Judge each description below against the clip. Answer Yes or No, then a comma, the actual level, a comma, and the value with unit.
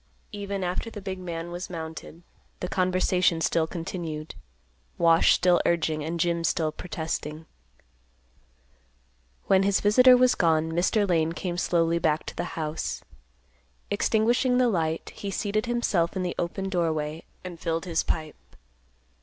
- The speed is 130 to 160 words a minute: Yes, average, 140 wpm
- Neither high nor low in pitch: Yes, medium, 175 Hz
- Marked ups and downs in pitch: No, average, 3.0 semitones